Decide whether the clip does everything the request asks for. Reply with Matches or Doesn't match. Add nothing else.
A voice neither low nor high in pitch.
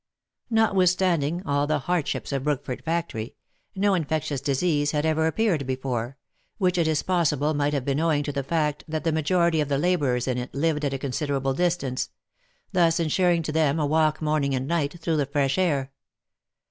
Matches